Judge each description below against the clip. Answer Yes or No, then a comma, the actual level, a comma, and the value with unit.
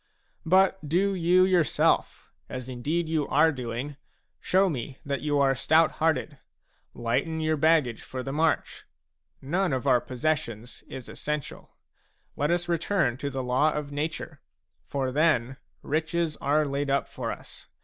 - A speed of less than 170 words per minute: Yes, average, 150 wpm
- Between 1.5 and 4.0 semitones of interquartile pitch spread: Yes, average, 3.6 semitones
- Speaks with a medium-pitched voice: Yes, medium, 150 Hz